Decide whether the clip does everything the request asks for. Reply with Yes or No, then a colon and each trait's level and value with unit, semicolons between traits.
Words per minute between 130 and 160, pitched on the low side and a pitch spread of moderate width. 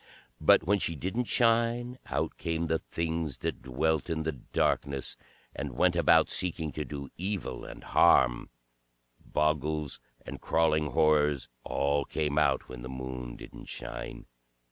Yes: average, 145 wpm; very low, 75 Hz; average, 3.0 semitones